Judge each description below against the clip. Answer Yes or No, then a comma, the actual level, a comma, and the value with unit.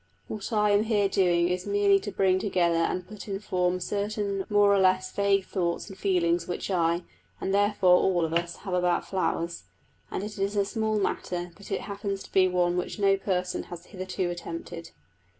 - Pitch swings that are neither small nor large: No, narrow, 2.2 semitones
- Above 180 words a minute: Yes, average, 195 wpm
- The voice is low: No, high, 190 Hz